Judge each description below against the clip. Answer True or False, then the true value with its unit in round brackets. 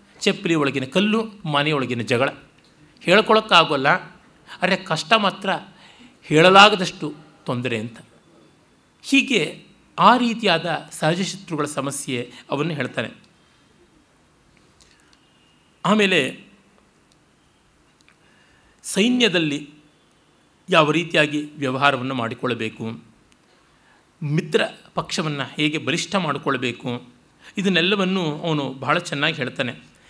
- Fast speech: False (70 wpm)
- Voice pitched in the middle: True (155 Hz)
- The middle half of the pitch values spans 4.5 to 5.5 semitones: True (5.2 semitones)